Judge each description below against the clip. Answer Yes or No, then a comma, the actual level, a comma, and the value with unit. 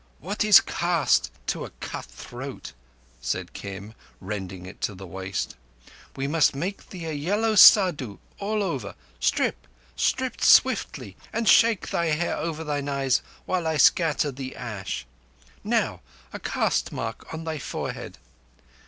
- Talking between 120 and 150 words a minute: Yes, average, 140 wpm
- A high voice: No, medium, 145 Hz